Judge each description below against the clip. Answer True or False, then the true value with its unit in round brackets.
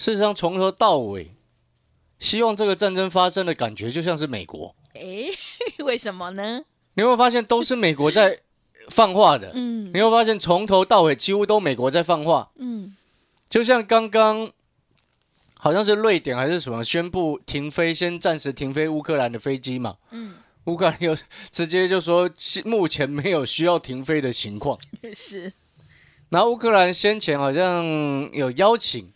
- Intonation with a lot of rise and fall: True (6.3 semitones)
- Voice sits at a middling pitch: True (180 Hz)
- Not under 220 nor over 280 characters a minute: True (250 characters per minute)